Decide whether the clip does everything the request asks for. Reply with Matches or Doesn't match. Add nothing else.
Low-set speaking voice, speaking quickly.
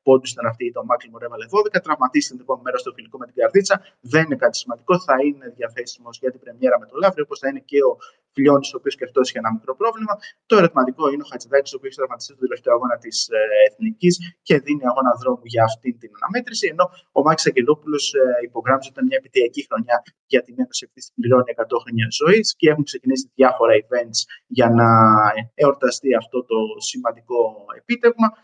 Doesn't match